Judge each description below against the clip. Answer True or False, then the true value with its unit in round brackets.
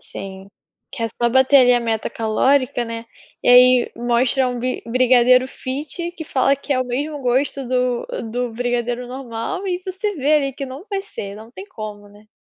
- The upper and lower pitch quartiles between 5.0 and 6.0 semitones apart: False (2.8 semitones)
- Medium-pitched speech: False (250 Hz)